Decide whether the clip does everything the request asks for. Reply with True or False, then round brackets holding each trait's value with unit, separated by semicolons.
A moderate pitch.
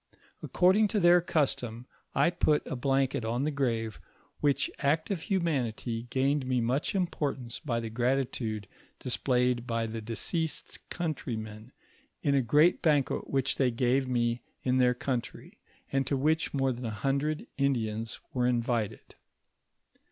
False (130 Hz)